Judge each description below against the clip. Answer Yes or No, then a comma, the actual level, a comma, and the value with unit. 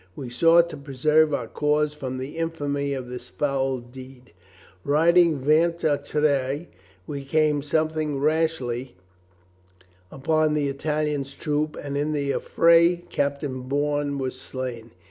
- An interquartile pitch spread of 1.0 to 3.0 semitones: Yes, narrow, 2.4 semitones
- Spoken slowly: Yes, slow, 130 wpm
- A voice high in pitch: No, medium, 145 Hz